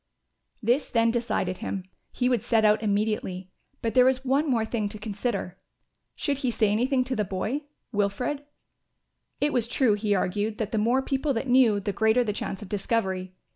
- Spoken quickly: No, average, 185 wpm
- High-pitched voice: Yes, high, 225 Hz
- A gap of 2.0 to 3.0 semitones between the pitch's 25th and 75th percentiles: No, average, 3.5 semitones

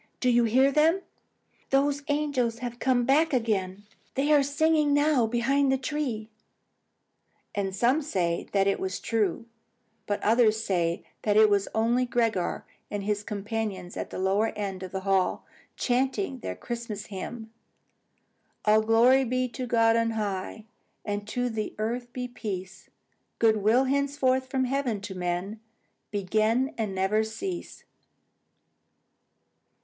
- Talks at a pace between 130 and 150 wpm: Yes, average, 140 wpm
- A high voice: Yes, high, 230 Hz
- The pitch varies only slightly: No, average, 4.2 semitones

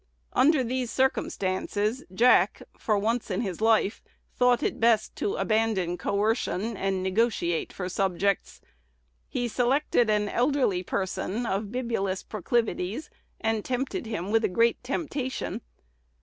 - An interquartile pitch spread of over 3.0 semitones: Yes, average, 4.0 semitones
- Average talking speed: No, slow, 125 wpm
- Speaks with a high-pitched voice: Yes, high, 220 Hz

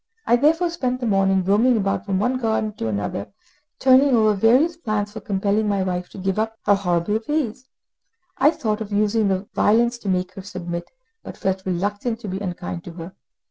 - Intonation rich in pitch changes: No, average, 3.8 semitones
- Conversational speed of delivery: Yes, average, 190 wpm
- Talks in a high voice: Yes, high, 205 Hz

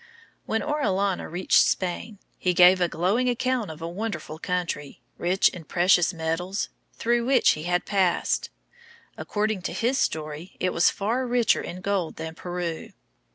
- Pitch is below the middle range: No, medium, 185 Hz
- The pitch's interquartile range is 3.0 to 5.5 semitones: Yes, average, 4.2 semitones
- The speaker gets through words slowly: No, average, 155 wpm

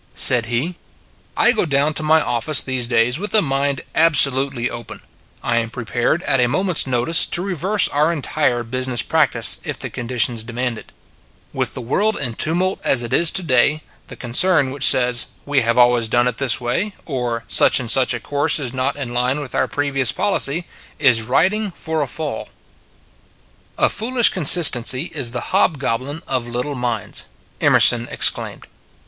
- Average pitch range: Yes, average, 4.3 semitones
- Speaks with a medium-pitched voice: No, low, 130 Hz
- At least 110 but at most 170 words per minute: No, average, 180 wpm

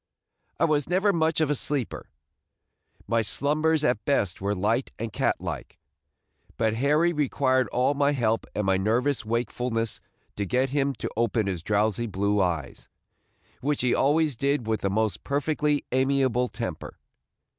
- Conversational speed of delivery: Yes, average, 155 wpm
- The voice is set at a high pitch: No, low, 125 Hz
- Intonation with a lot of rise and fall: No, average, 4.9 semitones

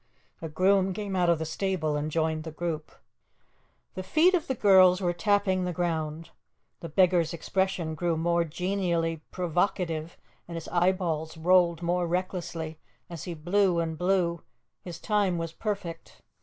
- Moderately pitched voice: Yes, medium, 175 Hz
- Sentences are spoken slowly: No, average, 155 wpm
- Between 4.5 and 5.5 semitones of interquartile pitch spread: No, narrow, 2.4 semitones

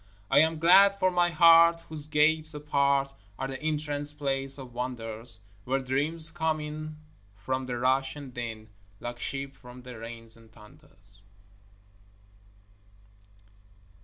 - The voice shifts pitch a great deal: No, average, 4.0 semitones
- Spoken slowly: Yes, slow, 130 wpm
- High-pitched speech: No, medium, 140 Hz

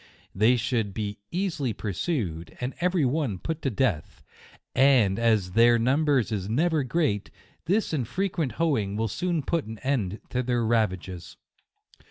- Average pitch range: No, wide, 6.3 semitones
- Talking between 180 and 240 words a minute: No, average, 150 wpm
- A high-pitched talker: No, low, 120 Hz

